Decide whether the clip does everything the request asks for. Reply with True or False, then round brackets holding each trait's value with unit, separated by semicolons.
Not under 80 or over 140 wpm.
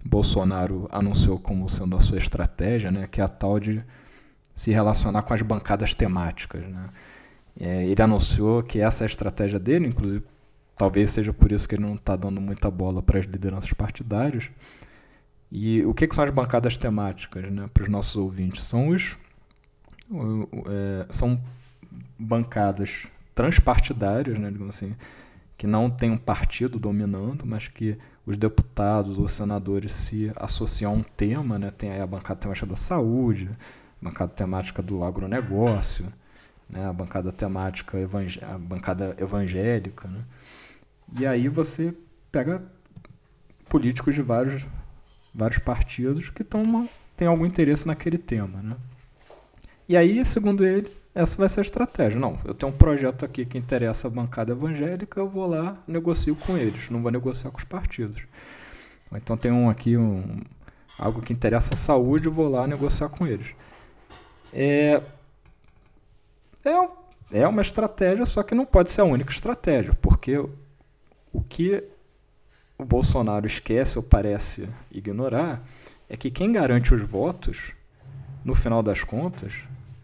False (150 wpm)